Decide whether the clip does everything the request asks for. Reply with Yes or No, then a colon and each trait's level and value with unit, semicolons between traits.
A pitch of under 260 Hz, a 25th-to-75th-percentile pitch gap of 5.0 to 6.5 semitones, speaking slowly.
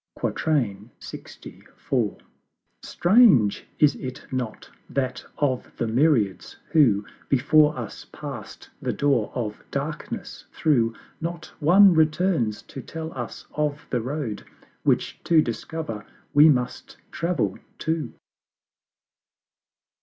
Yes: medium, 140 Hz; average, 5.3 semitones; slow, 100 wpm